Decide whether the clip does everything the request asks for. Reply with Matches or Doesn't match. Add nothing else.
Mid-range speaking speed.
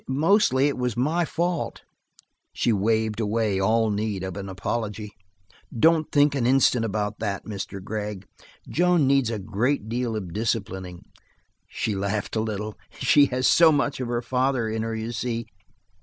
Matches